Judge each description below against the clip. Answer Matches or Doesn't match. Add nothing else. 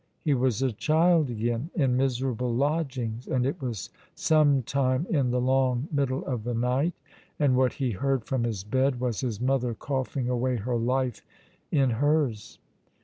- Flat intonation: Matches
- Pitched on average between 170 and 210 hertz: Doesn't match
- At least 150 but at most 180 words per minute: Matches